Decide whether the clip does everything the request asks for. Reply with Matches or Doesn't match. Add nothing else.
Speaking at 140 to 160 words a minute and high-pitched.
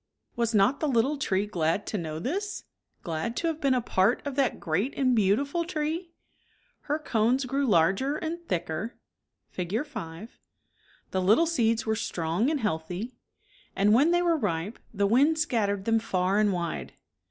Doesn't match